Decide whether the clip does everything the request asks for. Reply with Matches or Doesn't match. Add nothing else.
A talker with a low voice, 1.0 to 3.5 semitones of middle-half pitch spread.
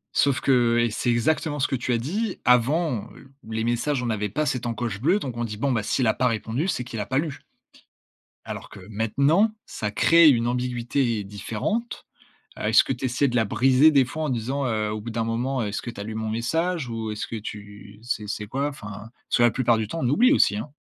Doesn't match